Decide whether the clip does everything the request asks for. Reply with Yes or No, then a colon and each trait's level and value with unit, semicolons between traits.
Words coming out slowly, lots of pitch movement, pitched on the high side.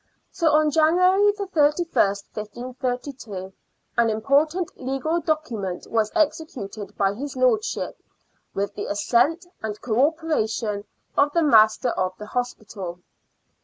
Yes: slow, 115 wpm; wide, 6.8 semitones; very high, 250 Hz